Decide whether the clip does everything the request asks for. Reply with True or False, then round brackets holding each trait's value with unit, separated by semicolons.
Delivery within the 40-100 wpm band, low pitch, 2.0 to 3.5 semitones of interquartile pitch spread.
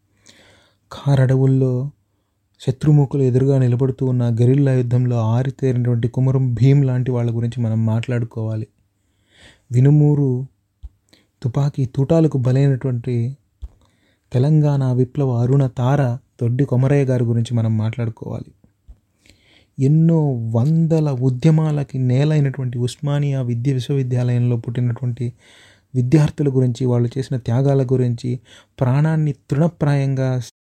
True (90 wpm; 125 Hz; 2.9 semitones)